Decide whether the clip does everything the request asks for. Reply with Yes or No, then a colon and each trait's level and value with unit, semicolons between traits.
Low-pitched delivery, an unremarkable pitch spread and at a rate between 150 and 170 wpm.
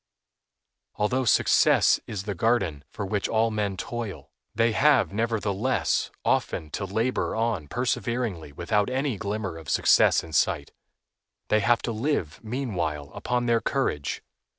No: low, 110 Hz; average, 3.9 semitones; slow, 135 wpm